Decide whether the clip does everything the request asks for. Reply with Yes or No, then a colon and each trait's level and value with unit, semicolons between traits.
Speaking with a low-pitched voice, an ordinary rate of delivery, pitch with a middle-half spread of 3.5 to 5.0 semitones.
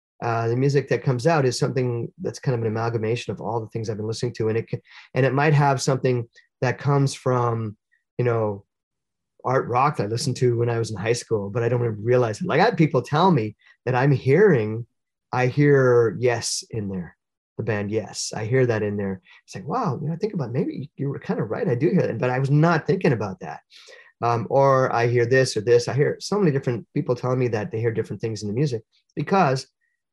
No: low, 125 Hz; fast, 245 wpm; average, 3.9 semitones